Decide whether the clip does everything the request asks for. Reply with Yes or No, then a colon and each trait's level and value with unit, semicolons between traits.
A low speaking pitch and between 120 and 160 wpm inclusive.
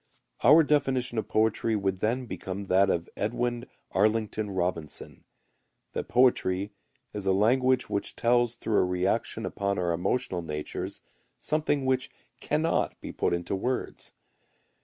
Yes: low, 110 Hz; slow, 135 wpm